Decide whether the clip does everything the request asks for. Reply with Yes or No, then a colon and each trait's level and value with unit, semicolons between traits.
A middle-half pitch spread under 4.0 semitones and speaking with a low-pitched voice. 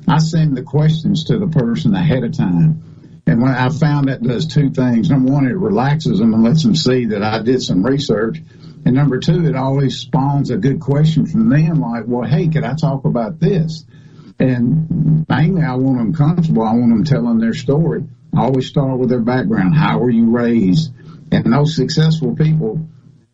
No: average, 3.6 semitones; medium, 150 Hz